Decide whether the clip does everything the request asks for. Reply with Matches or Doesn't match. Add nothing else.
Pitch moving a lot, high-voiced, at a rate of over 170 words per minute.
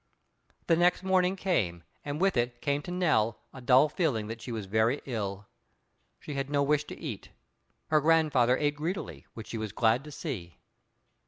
Doesn't match